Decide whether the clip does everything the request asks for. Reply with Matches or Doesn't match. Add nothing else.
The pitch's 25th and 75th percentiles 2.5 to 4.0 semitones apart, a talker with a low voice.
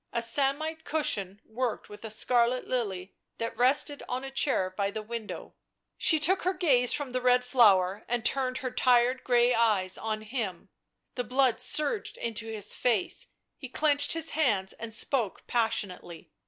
Doesn't match